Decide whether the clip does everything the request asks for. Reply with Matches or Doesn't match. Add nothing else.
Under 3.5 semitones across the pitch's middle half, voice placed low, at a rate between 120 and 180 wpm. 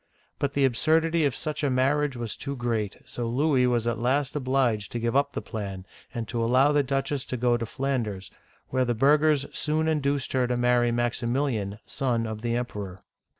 Doesn't match